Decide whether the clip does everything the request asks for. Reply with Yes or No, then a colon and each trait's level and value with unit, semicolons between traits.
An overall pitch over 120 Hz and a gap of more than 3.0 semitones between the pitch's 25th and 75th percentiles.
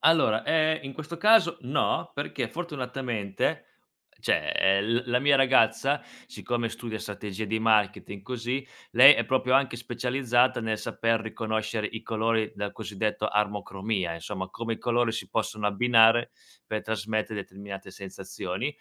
No: low, 115 Hz; average, 3.4 semitones